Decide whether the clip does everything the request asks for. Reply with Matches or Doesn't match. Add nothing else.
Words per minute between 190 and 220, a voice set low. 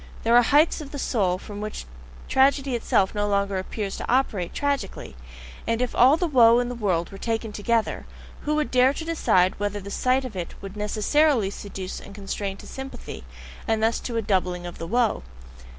Doesn't match